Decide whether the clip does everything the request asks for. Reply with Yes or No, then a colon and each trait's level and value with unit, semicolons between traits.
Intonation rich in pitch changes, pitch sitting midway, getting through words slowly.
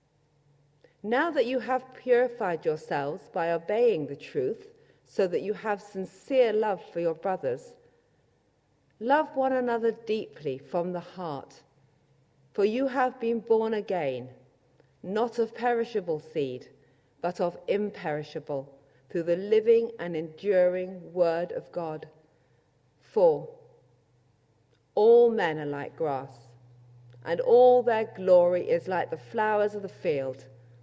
Yes: wide, 8.1 semitones; medium, 180 Hz; slow, 125 wpm